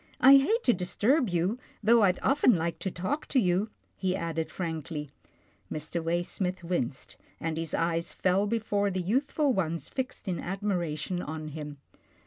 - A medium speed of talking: Yes, average, 155 wpm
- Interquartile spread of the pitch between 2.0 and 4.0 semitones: No, average, 4.6 semitones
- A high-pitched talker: No, medium, 180 Hz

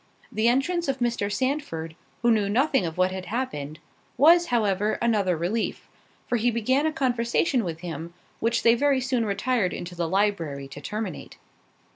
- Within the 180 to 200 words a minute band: No, average, 165 wpm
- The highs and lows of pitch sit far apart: Yes, wide, 5.9 semitones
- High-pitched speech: Yes, high, 225 Hz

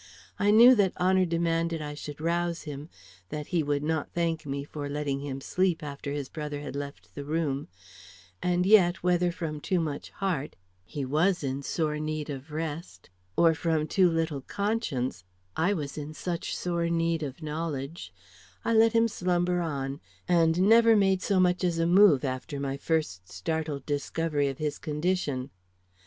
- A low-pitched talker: No, medium, 160 Hz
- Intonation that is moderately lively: Yes, average, 3.6 semitones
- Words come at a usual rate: Yes, average, 175 wpm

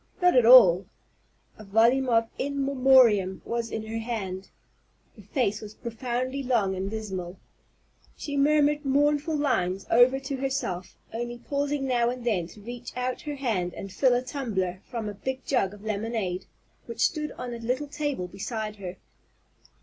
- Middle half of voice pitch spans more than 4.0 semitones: Yes, average, 4.7 semitones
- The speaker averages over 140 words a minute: Yes, average, 165 wpm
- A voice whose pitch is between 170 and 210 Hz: No, high, 235 Hz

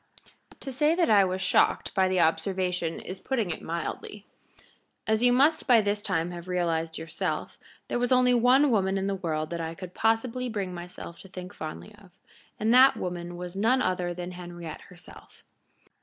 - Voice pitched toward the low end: No, medium, 185 Hz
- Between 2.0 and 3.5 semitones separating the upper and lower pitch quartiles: No, average, 4.5 semitones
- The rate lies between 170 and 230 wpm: Yes, average, 185 wpm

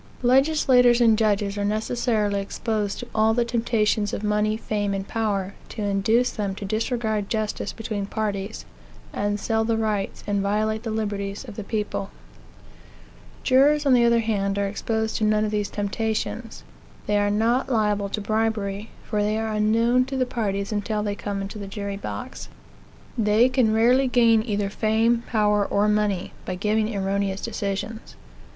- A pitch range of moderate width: No, narrow, 1.9 semitones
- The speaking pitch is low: No, high, 215 Hz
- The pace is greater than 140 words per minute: Yes, average, 165 wpm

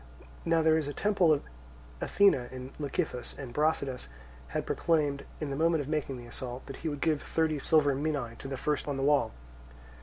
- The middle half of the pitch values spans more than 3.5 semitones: No, average, 2.8 semitones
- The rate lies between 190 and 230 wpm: Yes, fast, 205 wpm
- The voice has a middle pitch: Yes, medium, 145 Hz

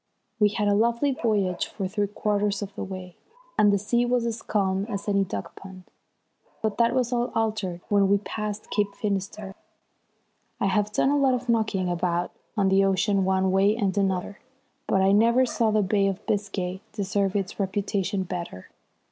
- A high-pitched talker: Yes, high, 200 Hz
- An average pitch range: No, narrow, 2.0 semitones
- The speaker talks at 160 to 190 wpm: Yes, average, 180 wpm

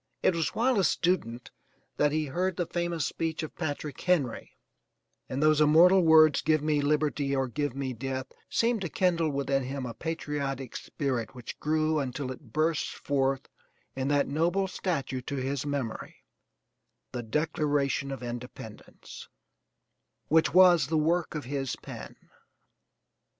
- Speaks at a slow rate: No, average, 145 wpm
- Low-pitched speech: No, medium, 145 Hz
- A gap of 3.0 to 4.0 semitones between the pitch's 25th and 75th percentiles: Yes, average, 3.3 semitones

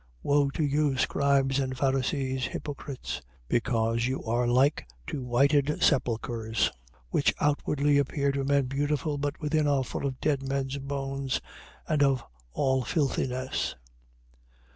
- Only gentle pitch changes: Yes, narrow, 1.7 semitones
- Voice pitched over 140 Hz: No, low, 135 Hz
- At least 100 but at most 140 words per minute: Yes, slow, 135 wpm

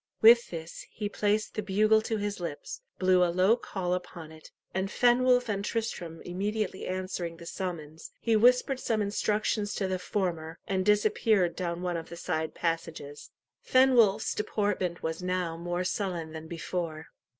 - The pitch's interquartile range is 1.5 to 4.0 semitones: Yes, average, 3.7 semitones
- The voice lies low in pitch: No, medium, 185 Hz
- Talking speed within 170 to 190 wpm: No, average, 160 wpm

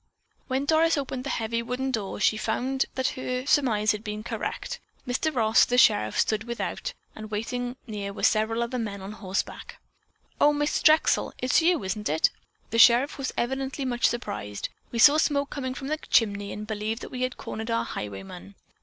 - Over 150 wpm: Yes, average, 185 wpm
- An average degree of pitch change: Yes, average, 3.9 semitones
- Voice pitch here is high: Yes, high, 235 Hz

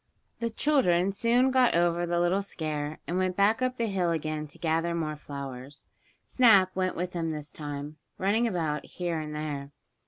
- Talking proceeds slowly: No, average, 180 wpm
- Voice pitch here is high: No, medium, 170 Hz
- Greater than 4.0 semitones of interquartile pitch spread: Yes, average, 4.5 semitones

